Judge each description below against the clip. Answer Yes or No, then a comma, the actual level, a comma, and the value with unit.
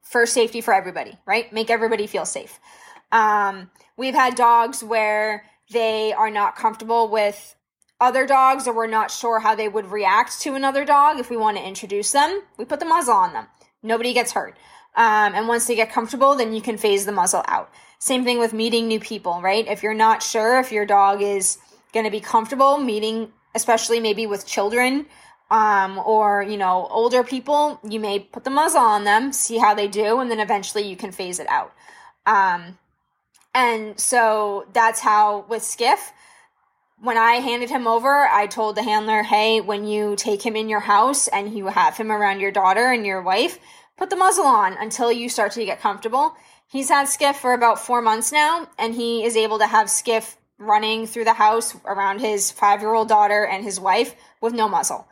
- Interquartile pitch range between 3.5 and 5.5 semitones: No, average, 2.9 semitones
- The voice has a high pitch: Yes, high, 225 Hz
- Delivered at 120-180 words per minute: No, average, 200 wpm